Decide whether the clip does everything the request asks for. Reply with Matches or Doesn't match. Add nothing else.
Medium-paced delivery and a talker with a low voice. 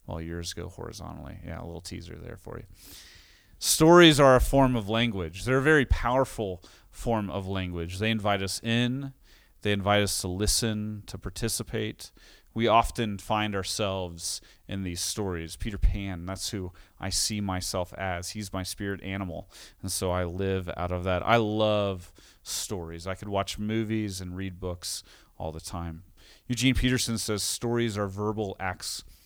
Matches